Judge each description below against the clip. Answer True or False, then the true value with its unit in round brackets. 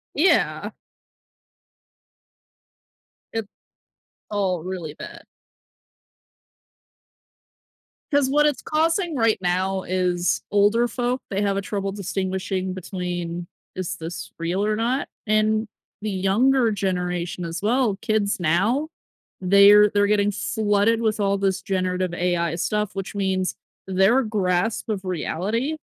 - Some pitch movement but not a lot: True (3.1 semitones)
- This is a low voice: False (200 Hz)